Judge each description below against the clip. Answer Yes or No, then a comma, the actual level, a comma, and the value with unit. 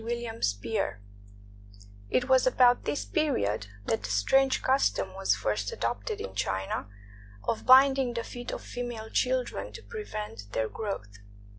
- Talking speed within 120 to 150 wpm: Yes, average, 140 wpm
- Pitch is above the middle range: Yes, high, 220 Hz